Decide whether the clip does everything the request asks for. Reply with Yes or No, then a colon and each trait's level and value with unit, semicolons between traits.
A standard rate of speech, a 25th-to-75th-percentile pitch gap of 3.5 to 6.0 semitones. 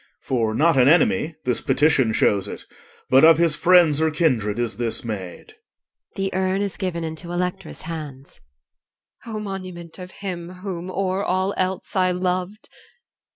Yes: average, 155 wpm; average, 5.1 semitones